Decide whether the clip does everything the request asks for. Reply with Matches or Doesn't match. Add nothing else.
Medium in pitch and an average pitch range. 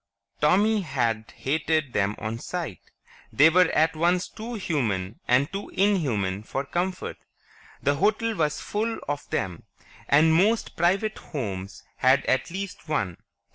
Doesn't match